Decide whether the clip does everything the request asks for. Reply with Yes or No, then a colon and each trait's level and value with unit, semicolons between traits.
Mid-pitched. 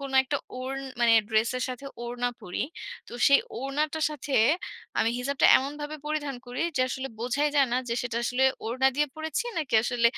No: very high, 265 Hz